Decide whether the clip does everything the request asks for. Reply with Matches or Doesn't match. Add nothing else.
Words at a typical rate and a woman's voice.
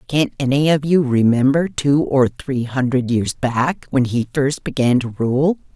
Matches